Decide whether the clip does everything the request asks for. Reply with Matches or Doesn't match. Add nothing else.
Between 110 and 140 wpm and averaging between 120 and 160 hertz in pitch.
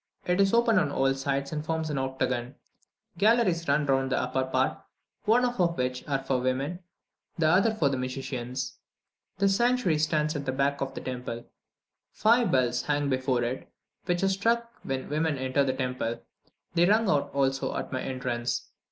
Doesn't match